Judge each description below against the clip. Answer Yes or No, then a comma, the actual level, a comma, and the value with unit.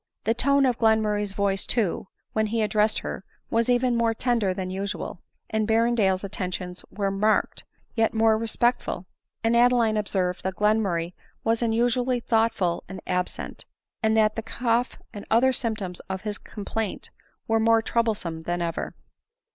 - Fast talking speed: No, average, 155 wpm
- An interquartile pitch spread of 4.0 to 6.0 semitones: No, average, 3.0 semitones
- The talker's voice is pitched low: No, high, 220 Hz